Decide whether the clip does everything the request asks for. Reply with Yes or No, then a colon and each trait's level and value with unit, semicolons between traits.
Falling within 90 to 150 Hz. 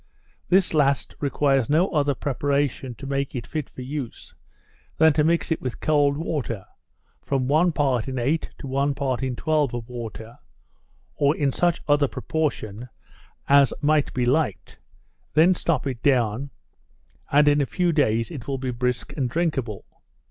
Yes: medium, 140 Hz